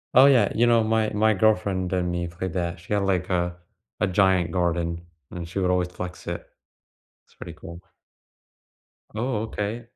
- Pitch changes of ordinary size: Yes, average, 3.7 semitones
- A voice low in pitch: Yes, very low, 95 Hz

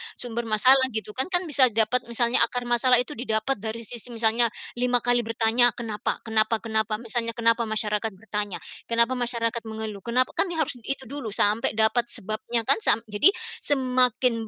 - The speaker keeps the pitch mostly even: Yes, narrow, 2.1 semitones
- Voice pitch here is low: No, high, 230 Hz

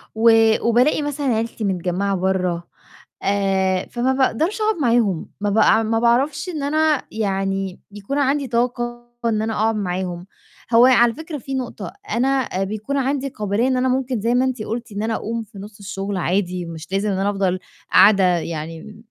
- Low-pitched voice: No, high, 220 Hz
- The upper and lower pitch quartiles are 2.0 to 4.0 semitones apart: No, average, 4.7 semitones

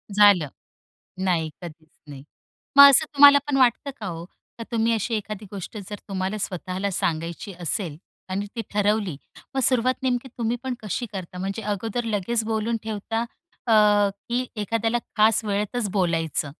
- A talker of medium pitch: No, high, 210 Hz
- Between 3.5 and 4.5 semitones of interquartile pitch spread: Yes, average, 3.8 semitones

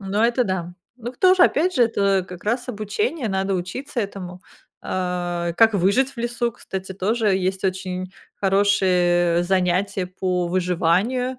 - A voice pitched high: Yes, high, 195 Hz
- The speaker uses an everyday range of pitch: Yes, average, 4.3 semitones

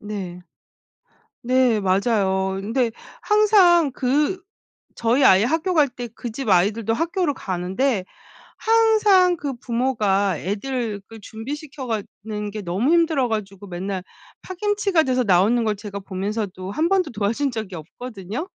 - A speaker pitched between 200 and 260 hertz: Yes, high, 230 Hz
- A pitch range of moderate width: No, wide, 6.7 semitones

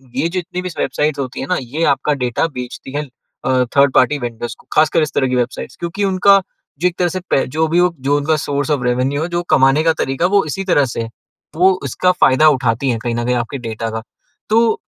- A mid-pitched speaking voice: Yes, medium, 145 Hz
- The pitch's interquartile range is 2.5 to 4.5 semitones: No, average, 5.2 semitones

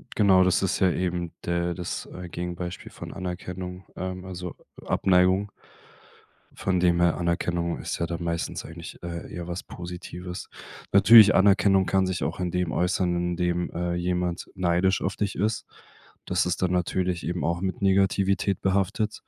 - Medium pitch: No, very low, 90 Hz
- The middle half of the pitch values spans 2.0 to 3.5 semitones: No, narrow, 1.5 semitones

